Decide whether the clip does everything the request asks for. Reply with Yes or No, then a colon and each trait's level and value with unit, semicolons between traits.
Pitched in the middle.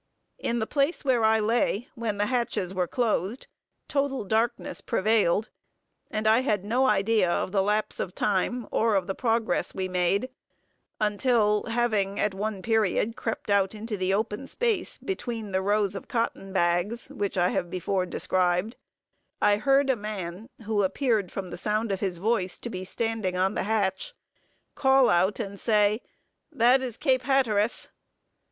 No: high, 215 Hz